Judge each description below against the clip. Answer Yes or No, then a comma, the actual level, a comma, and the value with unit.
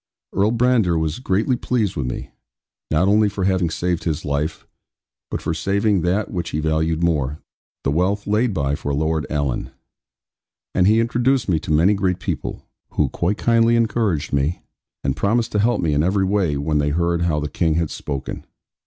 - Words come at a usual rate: Yes, average, 185 wpm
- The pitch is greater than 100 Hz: No, very low, 90 Hz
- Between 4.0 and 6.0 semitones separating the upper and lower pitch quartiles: Yes, average, 5.3 semitones